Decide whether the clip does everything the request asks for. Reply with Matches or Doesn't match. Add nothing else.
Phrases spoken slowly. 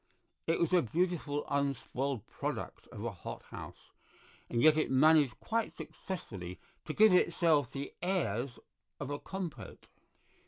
Matches